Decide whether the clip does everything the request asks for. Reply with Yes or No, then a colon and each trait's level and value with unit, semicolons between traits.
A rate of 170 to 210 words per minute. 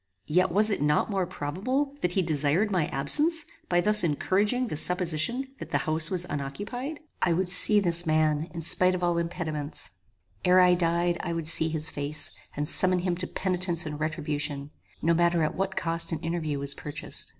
Yes: average, 190 wpm